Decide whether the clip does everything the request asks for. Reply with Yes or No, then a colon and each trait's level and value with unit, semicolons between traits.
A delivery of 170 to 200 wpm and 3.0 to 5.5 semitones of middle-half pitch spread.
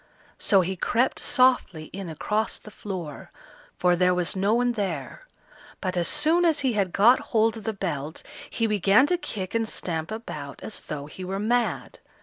Yes: average, 180 wpm; average, 4.5 semitones